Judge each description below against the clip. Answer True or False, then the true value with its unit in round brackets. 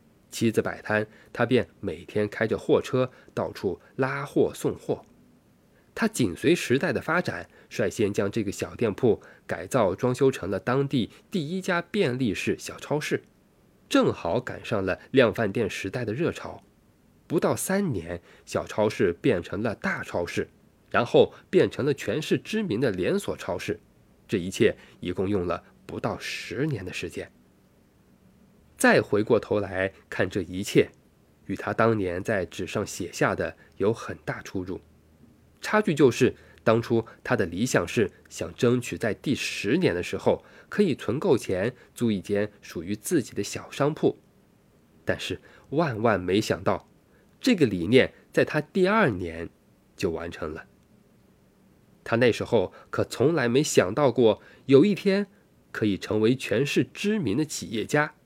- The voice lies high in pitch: False (110 Hz)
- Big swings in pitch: True (8.1 semitones)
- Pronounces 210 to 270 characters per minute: True (220 characters per minute)